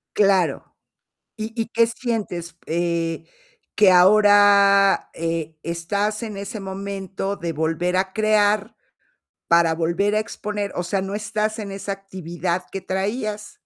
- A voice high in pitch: Yes, high, 195 Hz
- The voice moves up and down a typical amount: Yes, average, 3.2 semitones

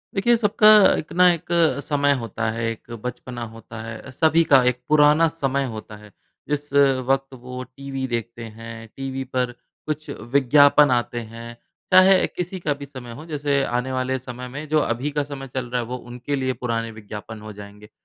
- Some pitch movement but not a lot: Yes, average, 3.6 semitones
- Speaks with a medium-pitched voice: No, low, 130 Hz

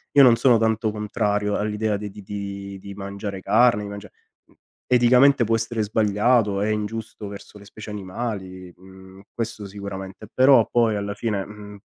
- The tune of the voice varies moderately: No, narrow, 2.2 semitones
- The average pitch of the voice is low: Yes, low, 105 Hz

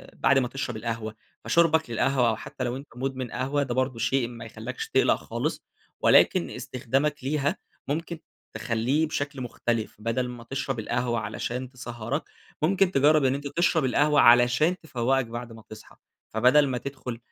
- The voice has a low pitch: Yes, low, 130 Hz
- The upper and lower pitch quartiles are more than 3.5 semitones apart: No, average, 3.2 semitones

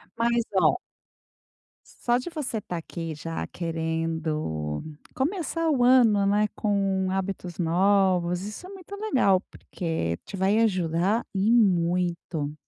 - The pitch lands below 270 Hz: Yes, high, 190 Hz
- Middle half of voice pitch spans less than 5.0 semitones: No, wide, 5.6 semitones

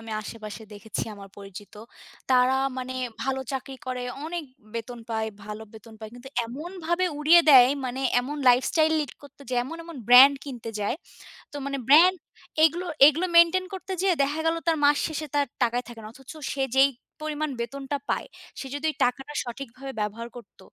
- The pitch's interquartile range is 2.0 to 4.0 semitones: No, average, 4.7 semitones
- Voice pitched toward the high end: Yes, very high, 270 Hz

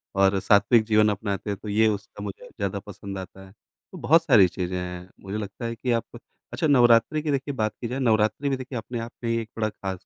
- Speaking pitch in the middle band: No, low, 110 Hz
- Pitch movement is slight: No, average, 3.3 semitones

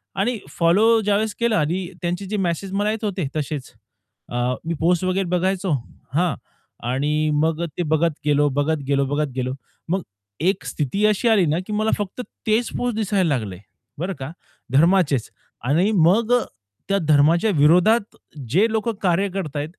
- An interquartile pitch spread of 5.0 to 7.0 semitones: Yes, average, 5.3 semitones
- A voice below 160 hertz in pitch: No, medium, 180 Hz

